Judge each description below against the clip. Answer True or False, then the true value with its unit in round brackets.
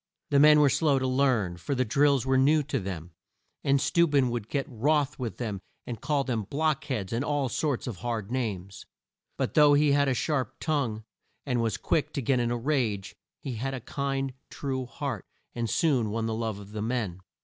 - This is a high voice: False (130 Hz)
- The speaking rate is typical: False (210 wpm)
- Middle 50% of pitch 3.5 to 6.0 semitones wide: True (4.0 semitones)